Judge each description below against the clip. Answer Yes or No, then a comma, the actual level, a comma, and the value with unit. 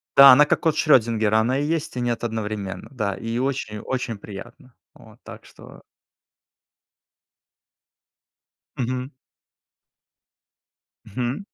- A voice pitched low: Yes, low, 120 Hz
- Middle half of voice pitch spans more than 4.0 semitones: No, average, 3.4 semitones